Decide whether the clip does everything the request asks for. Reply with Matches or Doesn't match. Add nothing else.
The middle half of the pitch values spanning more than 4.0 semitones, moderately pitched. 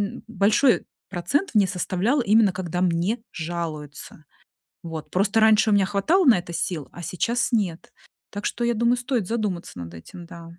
Doesn't match